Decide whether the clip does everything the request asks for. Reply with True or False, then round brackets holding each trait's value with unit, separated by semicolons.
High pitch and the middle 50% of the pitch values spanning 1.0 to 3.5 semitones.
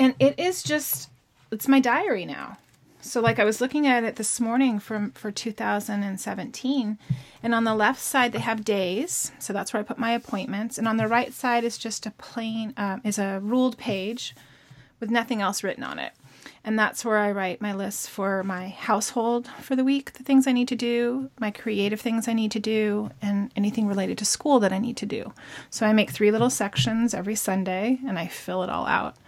True (220 Hz; 2.8 semitones)